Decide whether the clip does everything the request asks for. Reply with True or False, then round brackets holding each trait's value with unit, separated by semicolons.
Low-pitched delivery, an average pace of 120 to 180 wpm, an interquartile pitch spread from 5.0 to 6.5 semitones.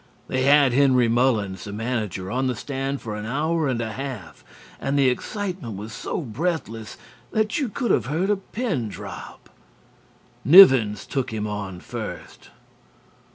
True (130 Hz; 155 wpm; 5.4 semitones)